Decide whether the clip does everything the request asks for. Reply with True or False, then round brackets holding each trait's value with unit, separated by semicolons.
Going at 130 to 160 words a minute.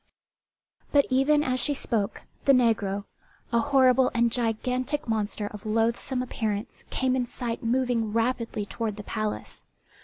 True (140 wpm)